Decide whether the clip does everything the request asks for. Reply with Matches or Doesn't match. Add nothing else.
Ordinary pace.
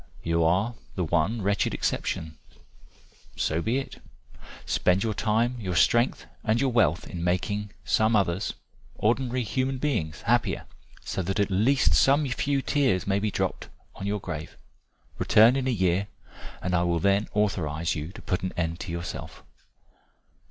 Matches